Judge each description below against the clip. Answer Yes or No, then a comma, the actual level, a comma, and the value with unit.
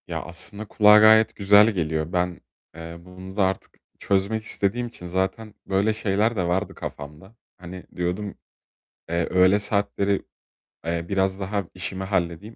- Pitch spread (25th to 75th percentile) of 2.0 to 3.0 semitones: Yes, average, 2.7 semitones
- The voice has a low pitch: Yes, very low, 95 Hz